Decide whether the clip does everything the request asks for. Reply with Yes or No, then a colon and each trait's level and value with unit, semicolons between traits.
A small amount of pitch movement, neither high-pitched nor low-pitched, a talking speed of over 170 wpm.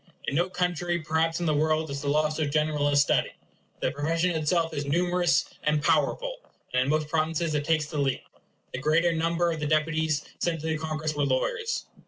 Yes: narrow, 2.0 semitones; medium, 155 Hz; fast, 205 wpm